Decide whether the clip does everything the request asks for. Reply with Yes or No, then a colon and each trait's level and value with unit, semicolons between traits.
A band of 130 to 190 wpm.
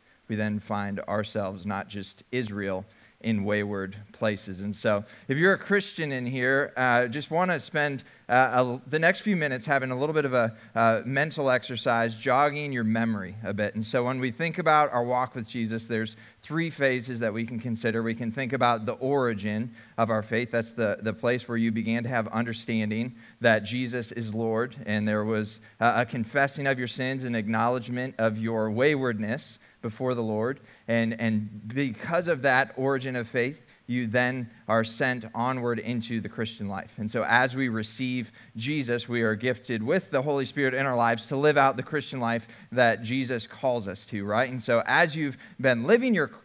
No: average, 200 wpm